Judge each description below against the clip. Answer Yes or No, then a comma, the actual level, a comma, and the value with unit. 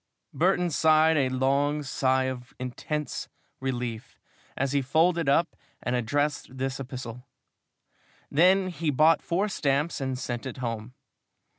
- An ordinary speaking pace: No, slow, 130 wpm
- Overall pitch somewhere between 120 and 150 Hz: Yes, low, 135 Hz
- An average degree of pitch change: Yes, average, 3.6 semitones